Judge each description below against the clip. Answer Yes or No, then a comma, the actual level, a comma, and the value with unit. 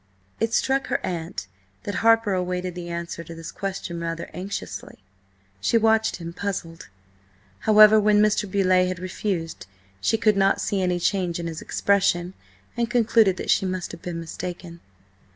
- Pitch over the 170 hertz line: Yes, medium, 185 Hz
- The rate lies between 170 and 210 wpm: No, average, 160 wpm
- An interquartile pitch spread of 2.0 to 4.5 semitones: Yes, average, 3.5 semitones